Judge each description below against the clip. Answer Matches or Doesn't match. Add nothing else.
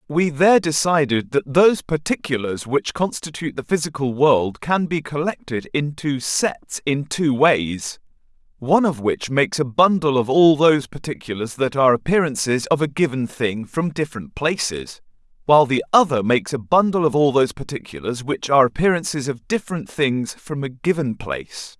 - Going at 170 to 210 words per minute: Doesn't match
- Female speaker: Doesn't match